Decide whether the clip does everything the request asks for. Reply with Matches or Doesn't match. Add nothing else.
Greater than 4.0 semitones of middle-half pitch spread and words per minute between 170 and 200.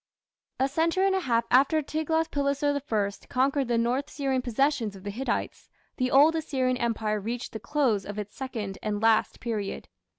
Matches